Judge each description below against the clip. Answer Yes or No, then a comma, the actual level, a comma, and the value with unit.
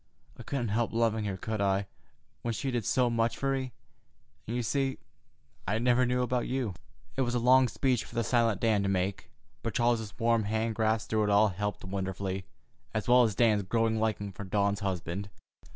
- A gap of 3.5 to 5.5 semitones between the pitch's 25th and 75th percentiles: No, average, 3.1 semitones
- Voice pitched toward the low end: Yes, low, 110 Hz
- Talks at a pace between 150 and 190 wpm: No, average, 200 wpm